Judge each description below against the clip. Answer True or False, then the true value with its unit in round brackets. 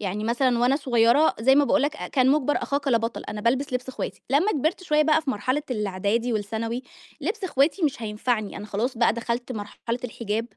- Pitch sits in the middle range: False (245 Hz)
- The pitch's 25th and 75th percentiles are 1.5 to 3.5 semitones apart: False (3.9 semitones)